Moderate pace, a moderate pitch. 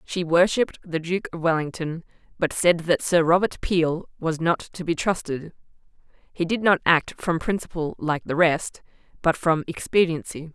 Yes: average, 165 wpm; medium, 170 Hz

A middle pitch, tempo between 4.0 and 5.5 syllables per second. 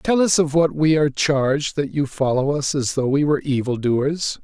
Yes: medium, 145 Hz; 5.0 syllables/s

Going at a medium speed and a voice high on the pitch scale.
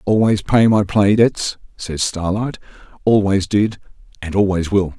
No: average, 145 wpm; low, 100 Hz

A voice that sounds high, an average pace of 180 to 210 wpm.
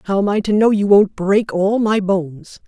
No: high, 200 Hz; fast, 245 wpm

